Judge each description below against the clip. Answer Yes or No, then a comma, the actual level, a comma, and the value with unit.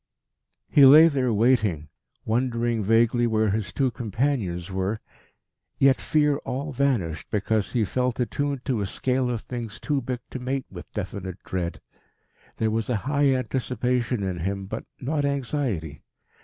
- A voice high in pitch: No, low, 120 Hz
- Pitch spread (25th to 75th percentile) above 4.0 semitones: Yes, average, 4.5 semitones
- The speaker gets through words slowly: No, average, 145 wpm